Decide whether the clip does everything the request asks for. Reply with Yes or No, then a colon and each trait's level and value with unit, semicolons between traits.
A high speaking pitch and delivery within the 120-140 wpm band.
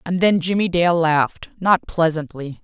No: medium, 170 Hz; slow, 135 wpm